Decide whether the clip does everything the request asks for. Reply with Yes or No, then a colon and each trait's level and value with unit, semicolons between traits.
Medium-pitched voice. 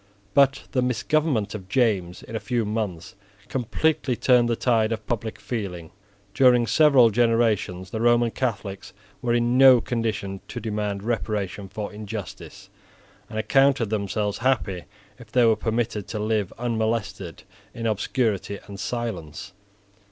No: low, 110 Hz